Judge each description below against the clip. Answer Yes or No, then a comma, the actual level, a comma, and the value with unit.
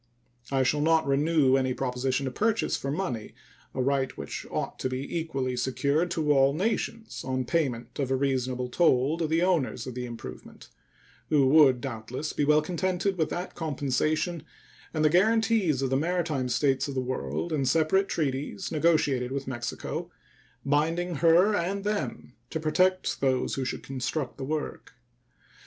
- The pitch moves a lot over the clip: No, average, 4.2 semitones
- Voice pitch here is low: No, medium, 145 Hz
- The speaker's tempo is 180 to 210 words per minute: No, average, 165 wpm